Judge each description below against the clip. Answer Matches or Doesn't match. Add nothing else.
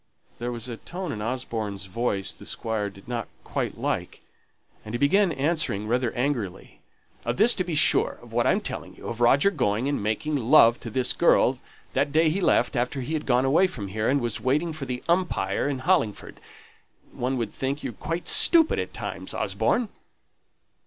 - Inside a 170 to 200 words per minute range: Matches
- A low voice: Matches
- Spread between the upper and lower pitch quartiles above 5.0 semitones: Matches